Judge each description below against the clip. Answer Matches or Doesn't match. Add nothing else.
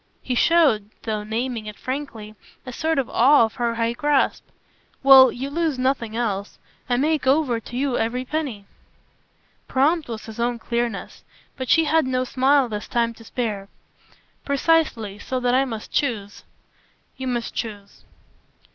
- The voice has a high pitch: Matches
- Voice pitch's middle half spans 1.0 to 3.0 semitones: Doesn't match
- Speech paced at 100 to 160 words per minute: Matches